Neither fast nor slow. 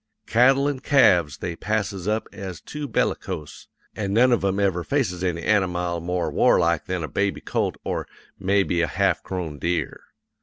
Yes: average, 165 wpm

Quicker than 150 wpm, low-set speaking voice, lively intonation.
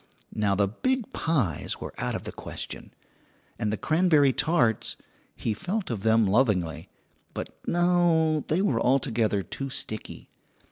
No: average, 140 wpm; low, 130 Hz; wide, 7.4 semitones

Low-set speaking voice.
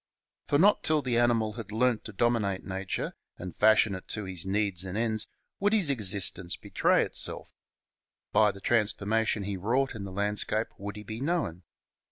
Yes: low, 105 Hz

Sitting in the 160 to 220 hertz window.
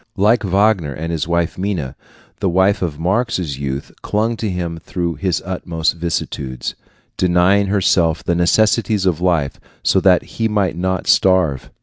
No: very low, 90 Hz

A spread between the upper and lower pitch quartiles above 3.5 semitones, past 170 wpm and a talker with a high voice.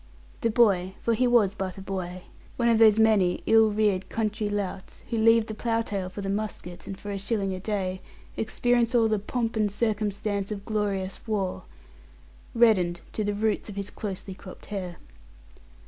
No: narrow, 2.4 semitones; average, 180 wpm; high, 205 Hz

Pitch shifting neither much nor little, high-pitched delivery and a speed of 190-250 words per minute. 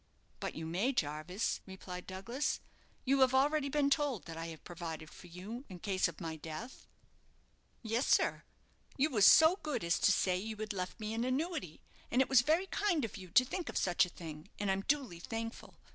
No: wide, 7.1 semitones; high, 215 Hz; fast, 205 wpm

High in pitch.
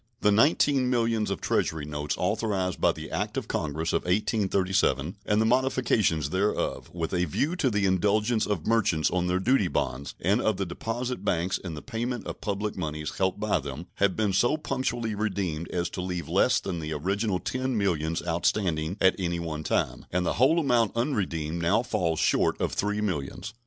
No: very low, 95 Hz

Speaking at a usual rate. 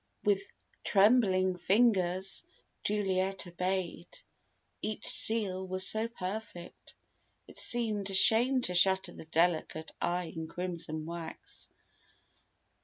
No: slow, 105 wpm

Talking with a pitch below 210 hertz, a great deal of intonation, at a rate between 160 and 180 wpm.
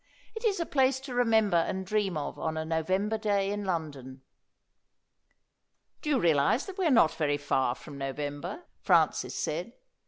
Yes: high, 190 Hz; wide, 8.6 semitones; average, 165 wpm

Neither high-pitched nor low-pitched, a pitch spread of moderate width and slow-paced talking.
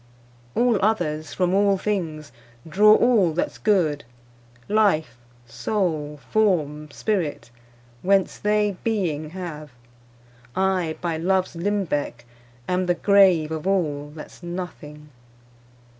Yes: medium, 180 Hz; average, 4.6 semitones; slow, 105 wpm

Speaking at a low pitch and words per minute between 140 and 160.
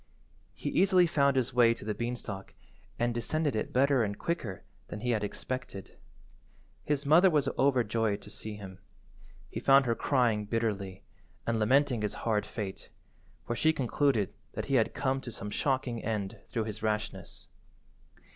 Yes: low, 120 Hz; average, 155 wpm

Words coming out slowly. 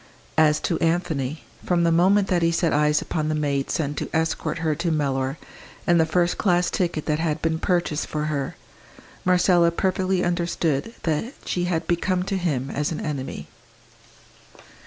No: average, 170 wpm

